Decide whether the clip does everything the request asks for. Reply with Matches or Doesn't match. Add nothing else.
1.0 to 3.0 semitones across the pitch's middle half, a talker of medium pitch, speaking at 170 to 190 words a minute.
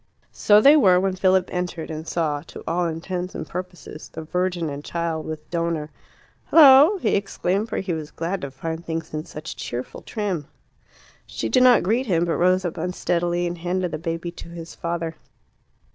Matches